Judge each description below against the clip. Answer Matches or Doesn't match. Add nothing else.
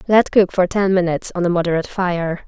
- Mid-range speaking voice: Matches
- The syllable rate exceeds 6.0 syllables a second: Matches